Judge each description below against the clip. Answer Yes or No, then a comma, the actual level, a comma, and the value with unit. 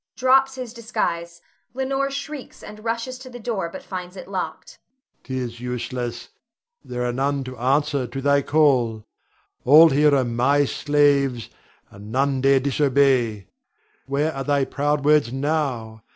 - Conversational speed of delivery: Yes, average, 145 wpm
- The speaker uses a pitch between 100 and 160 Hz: Yes, medium, 140 Hz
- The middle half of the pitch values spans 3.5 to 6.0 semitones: Yes, average, 5.0 semitones